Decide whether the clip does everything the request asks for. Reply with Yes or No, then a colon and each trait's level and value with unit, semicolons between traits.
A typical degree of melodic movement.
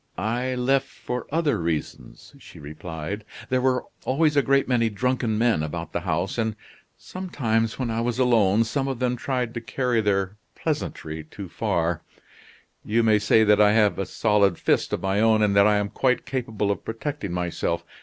Yes: average, 4.0 semitones